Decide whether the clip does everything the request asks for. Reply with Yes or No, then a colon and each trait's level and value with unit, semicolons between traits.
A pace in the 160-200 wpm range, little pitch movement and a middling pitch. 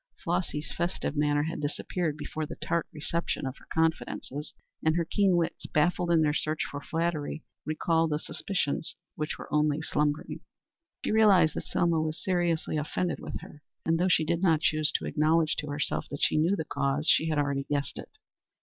Yes: average, 185 wpm; narrow, 2.2 semitones; medium, 155 Hz